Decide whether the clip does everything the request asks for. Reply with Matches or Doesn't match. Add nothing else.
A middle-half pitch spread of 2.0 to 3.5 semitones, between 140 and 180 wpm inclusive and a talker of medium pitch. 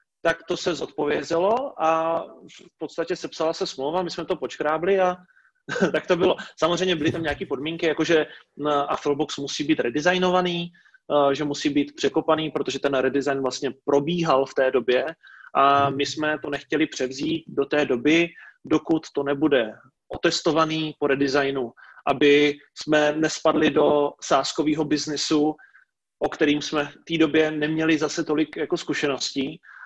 Matches